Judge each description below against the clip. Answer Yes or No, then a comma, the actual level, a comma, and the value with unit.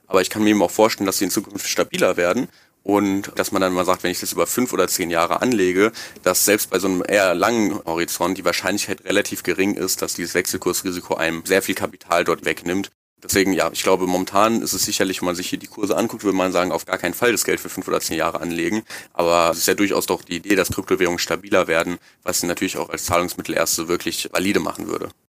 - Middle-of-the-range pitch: No, very low, 90 Hz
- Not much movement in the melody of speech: Yes, narrow, 1.9 semitones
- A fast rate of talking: Yes, fast, 245 wpm